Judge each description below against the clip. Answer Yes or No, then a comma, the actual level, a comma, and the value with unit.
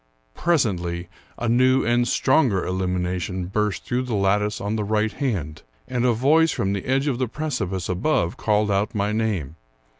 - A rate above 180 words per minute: No, average, 170 wpm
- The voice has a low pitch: Yes, low, 105 Hz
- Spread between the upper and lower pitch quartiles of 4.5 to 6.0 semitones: Yes, average, 5.1 semitones